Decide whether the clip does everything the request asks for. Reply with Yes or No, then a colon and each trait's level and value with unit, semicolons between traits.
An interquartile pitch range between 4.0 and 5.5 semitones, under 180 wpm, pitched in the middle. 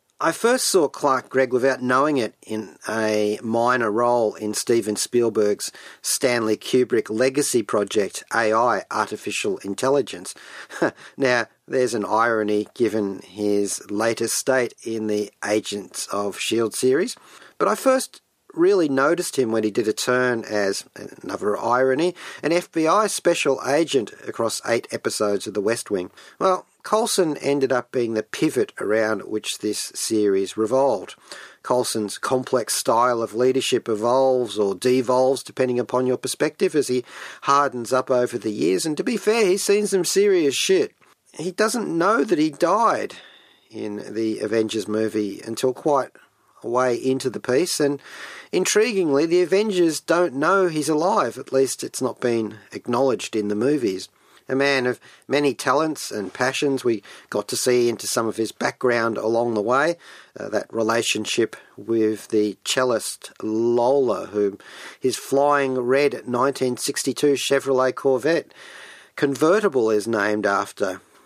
No: average, 4.8 semitones; average, 145 wpm; low, 125 Hz